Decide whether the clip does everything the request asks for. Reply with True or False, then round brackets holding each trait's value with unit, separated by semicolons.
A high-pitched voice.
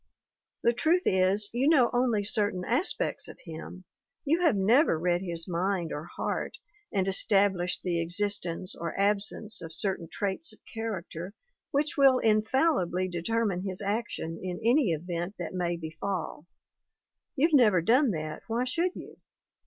True (200 Hz)